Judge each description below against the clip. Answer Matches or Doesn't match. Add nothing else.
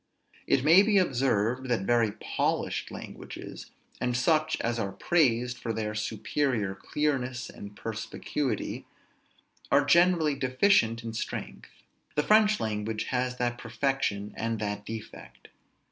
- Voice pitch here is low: Matches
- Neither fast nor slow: Doesn't match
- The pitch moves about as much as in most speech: Matches